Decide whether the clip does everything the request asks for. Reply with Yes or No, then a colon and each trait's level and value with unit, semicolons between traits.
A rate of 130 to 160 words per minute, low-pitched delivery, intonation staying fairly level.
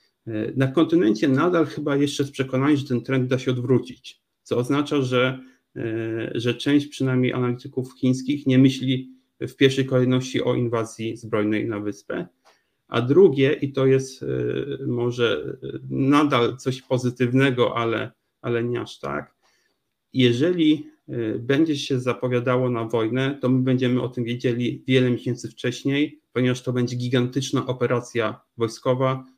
Yes: average, 135 wpm; low, 130 Hz; narrow, 2.0 semitones